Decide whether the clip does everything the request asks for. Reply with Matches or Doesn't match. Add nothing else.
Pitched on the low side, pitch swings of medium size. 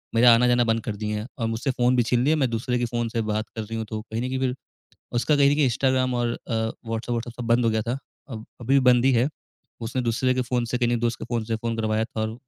Doesn't match